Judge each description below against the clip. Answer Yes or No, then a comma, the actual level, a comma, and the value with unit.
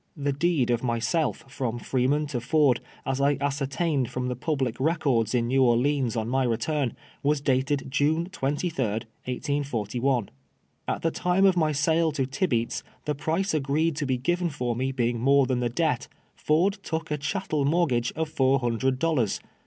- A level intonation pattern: No, average, 3.8 semitones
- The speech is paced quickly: No, average, 175 wpm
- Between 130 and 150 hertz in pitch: Yes, low, 135 Hz